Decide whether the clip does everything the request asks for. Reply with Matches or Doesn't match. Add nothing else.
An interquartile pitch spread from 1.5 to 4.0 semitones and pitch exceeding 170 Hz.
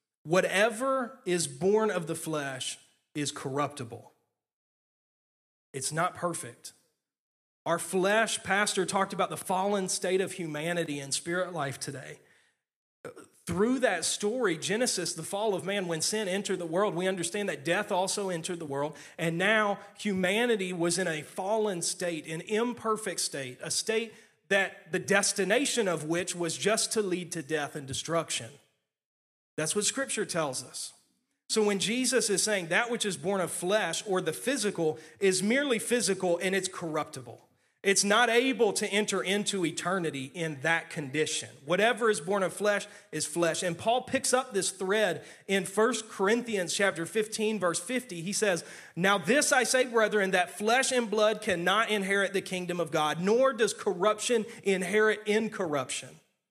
Doesn't match